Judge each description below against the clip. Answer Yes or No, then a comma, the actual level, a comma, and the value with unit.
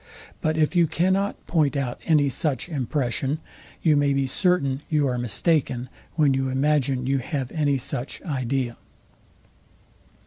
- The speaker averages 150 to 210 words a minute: No, average, 140 wpm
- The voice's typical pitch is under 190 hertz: Yes, medium, 140 Hz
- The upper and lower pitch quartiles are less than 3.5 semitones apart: Yes, average, 3.0 semitones